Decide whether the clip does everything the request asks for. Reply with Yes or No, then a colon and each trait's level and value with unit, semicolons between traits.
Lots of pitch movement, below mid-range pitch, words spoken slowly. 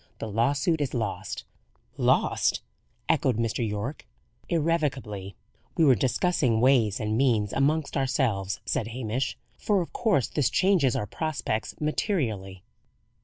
Yes: wide, 5.8 semitones; low, 130 Hz; slow, 120 wpm